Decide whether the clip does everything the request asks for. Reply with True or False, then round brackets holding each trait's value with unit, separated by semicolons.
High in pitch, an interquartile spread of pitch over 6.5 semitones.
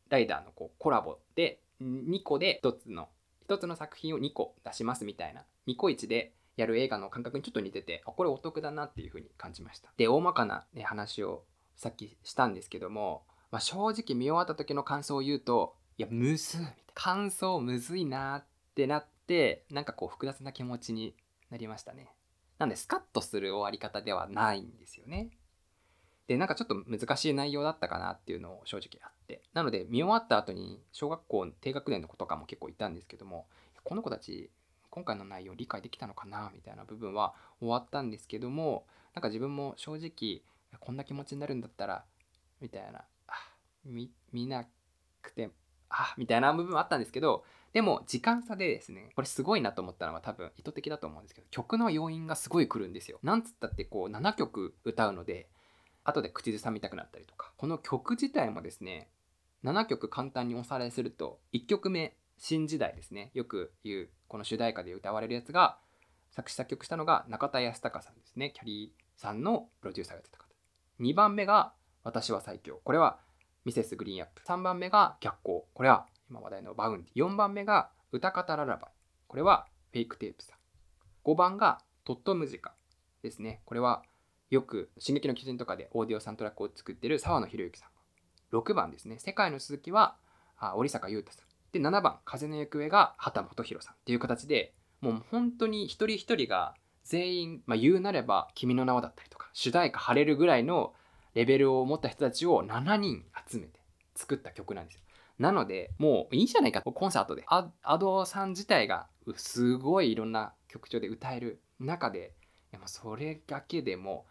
False (140 Hz; 7.1 semitones)